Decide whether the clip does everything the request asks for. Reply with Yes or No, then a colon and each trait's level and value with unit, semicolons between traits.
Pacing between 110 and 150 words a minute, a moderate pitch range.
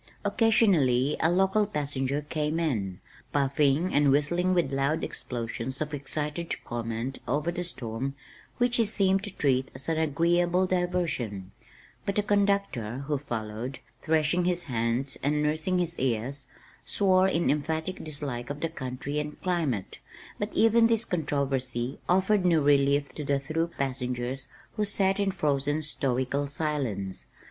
Yes: average, 140 wpm; average, 5.0 semitones